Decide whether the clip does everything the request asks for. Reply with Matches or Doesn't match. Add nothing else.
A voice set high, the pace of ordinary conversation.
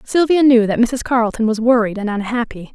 Matches